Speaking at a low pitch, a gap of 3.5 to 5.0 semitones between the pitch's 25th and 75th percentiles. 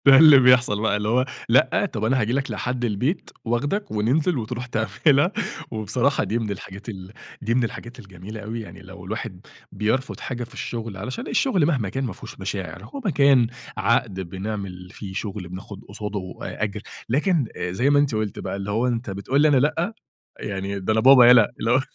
Yes: low, 115 Hz; average, 4.6 semitones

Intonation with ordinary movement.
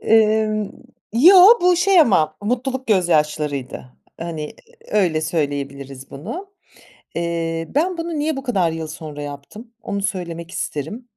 No: wide, 8.1 semitones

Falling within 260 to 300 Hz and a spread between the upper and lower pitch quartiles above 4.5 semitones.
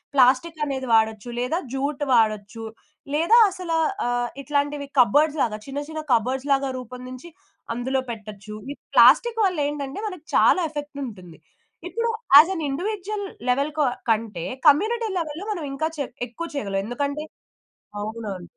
Yes: very high, 280 Hz; average, 5.2 semitones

